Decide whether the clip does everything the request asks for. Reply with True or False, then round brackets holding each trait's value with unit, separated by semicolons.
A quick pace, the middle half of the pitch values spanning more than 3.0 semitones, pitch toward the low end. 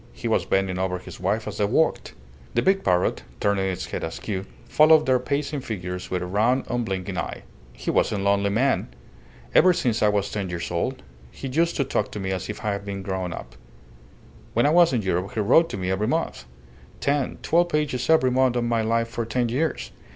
True (215 wpm; 5.6 semitones; 110 Hz)